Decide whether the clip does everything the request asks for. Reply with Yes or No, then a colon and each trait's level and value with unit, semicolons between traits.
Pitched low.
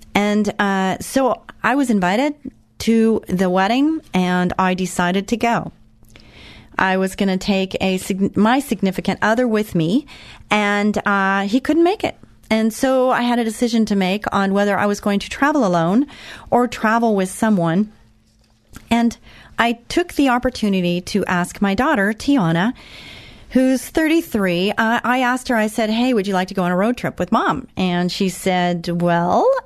No: high, 205 Hz